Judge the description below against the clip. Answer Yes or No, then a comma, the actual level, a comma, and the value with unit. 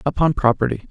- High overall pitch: No, low, 135 Hz